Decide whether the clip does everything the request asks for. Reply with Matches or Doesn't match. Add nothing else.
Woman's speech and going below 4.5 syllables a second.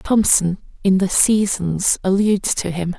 Matches